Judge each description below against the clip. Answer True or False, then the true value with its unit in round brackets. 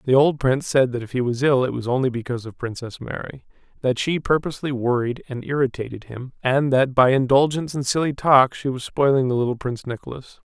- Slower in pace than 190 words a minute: False (205 wpm)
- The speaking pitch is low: True (130 Hz)